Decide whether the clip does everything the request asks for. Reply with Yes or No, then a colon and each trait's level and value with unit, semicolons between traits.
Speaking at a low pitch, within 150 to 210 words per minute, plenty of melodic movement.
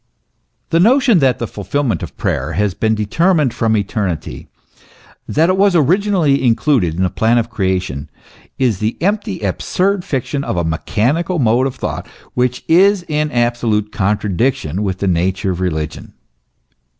Yes: low, 115 Hz; average, 155 wpm; wide, 7.9 semitones